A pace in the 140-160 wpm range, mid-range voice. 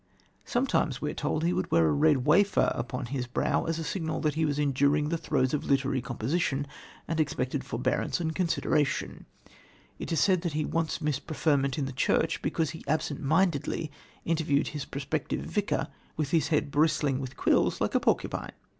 No: average, 180 wpm; medium, 150 Hz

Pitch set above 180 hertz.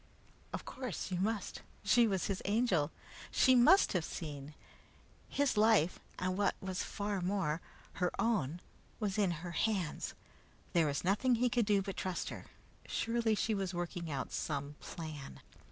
Yes: high, 190 Hz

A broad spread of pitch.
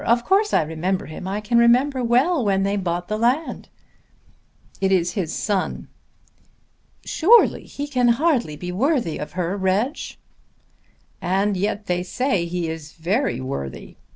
Yes: wide, 5.8 semitones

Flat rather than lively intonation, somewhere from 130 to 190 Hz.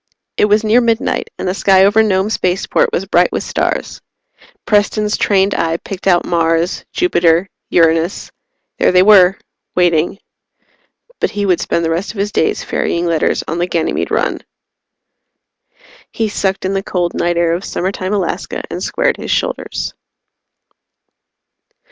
No: average, 3.1 semitones; medium, 185 Hz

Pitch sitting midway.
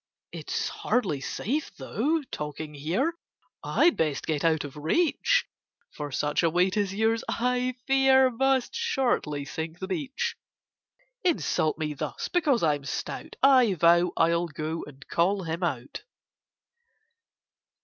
Yes: medium, 180 Hz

